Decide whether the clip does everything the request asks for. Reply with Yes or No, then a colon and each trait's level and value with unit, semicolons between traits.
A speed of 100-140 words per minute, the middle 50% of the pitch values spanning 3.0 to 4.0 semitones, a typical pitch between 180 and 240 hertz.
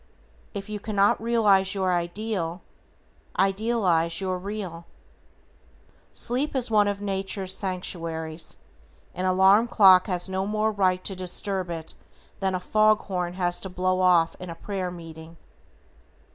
No: slow, 135 wpm; narrow, 2.4 semitones; high, 190 Hz